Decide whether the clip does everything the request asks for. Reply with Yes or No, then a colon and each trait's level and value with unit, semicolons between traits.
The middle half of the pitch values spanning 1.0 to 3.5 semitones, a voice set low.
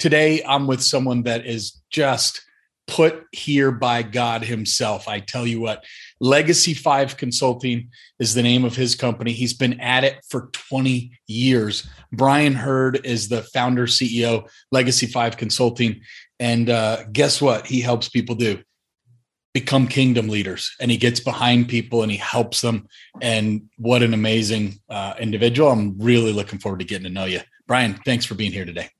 Yes: narrow, 2.4 semitones; low, 120 Hz